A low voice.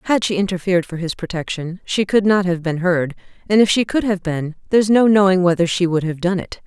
No: medium, 185 Hz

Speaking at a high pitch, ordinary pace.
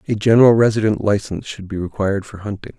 No: low, 105 Hz; average, 195 wpm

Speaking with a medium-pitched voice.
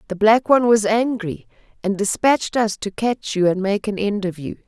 No: high, 210 Hz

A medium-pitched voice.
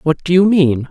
Yes: medium, 165 Hz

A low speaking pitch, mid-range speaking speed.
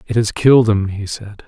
No: low, 105 Hz; fast, 245 wpm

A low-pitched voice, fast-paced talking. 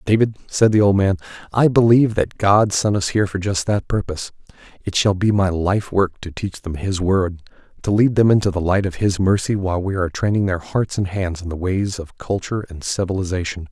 Yes: very low, 95 Hz; fast, 215 wpm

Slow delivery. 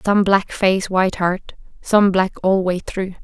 No: average, 185 wpm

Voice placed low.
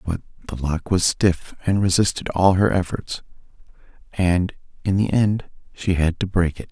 Yes: very low, 90 Hz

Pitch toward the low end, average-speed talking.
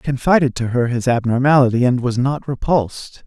Yes: low, 130 Hz; average, 185 wpm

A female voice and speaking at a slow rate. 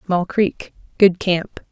Yes: female; slow, 105 wpm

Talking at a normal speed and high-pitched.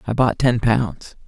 No: average, 190 wpm; low, 110 Hz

